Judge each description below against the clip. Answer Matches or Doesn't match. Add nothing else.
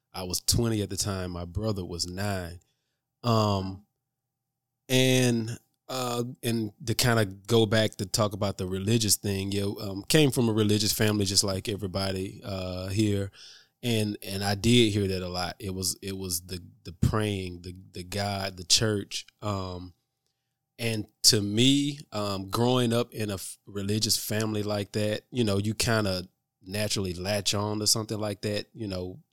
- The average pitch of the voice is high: Doesn't match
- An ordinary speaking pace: Matches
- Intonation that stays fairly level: Doesn't match